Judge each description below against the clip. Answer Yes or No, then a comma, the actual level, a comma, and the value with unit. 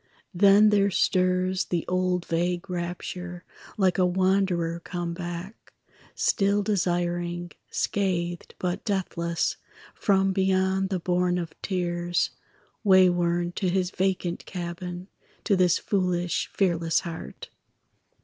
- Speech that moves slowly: Yes, slow, 110 wpm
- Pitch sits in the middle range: Yes, medium, 180 Hz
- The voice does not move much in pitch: Yes, narrow, 1.6 semitones